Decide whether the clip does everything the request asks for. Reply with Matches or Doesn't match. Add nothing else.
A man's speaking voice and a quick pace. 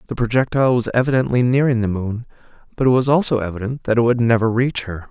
Matches